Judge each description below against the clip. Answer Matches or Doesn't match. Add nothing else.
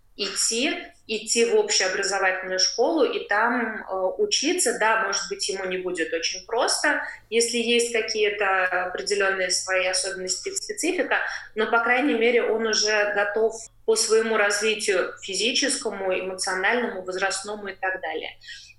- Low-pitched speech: Doesn't match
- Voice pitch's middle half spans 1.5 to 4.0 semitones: Matches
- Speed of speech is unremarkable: Matches